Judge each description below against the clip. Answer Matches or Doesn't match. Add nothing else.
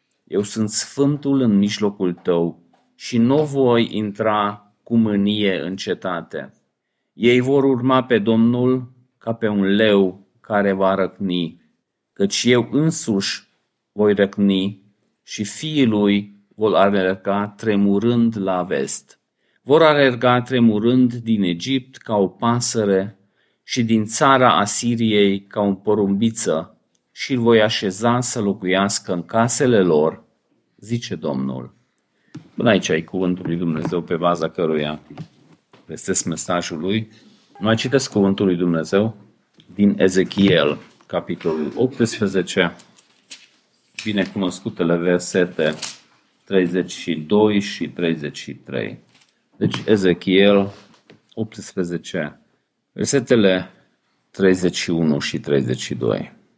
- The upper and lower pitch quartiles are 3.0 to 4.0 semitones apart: Matches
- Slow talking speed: Matches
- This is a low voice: Matches